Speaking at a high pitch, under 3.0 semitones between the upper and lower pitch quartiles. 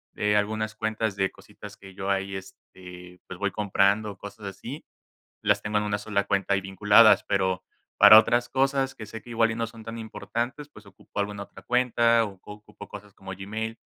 No: low, 105 Hz; narrow, 2.4 semitones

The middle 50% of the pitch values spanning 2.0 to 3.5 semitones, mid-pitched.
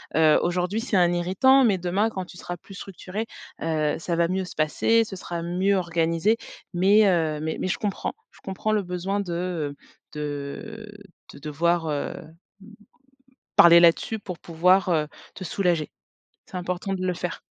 Yes: average, 2.8 semitones; medium, 180 Hz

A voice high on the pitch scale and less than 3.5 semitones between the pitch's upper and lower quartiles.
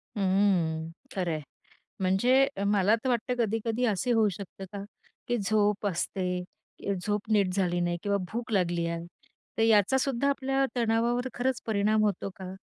No: high, 205 Hz; average, 3.9 semitones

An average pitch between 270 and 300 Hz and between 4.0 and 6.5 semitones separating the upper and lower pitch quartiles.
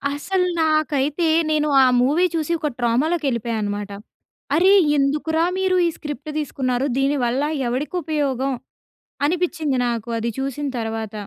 Yes: very high, 285 Hz; average, 4.3 semitones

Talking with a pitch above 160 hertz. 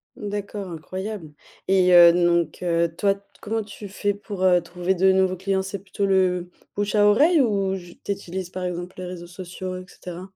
Yes: medium, 185 Hz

